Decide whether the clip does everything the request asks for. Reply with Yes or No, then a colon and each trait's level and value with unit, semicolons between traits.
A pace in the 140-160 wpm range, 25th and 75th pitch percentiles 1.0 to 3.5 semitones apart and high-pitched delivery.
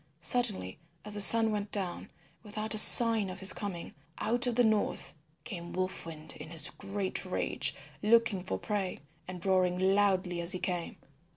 No: average, 170 wpm; average, 2.9 semitones; high, 195 Hz